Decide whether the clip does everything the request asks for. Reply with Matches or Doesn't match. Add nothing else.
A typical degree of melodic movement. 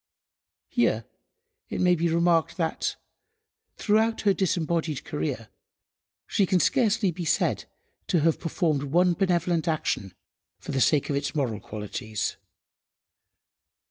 Matches